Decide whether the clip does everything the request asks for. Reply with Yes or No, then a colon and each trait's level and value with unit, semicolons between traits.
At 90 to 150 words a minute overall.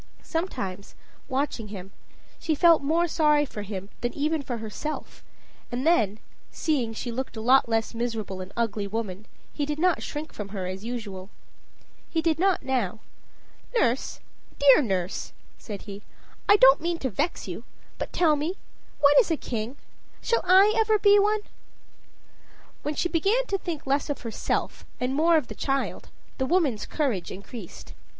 No: average, 160 wpm